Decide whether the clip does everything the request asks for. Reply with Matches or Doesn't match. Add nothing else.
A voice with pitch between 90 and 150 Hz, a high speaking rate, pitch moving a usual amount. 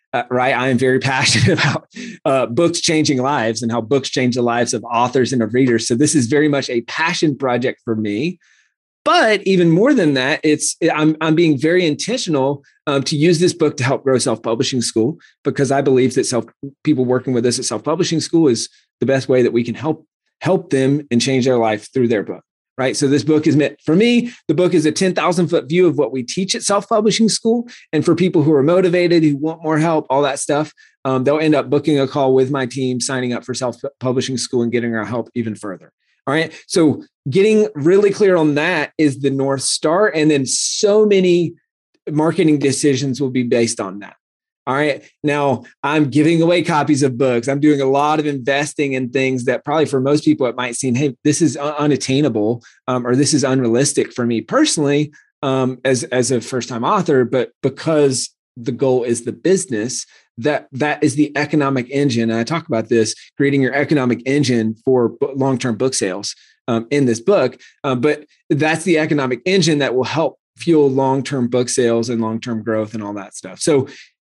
Matches